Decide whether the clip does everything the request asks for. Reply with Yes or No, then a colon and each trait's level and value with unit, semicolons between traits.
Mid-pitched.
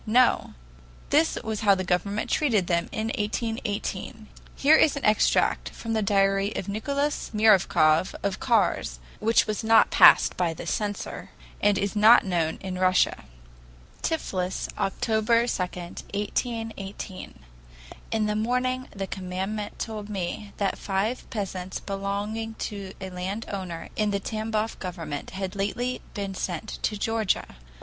No: high, 205 Hz